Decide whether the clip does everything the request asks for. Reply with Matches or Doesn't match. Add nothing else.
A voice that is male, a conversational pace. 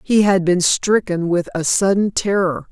Doesn't match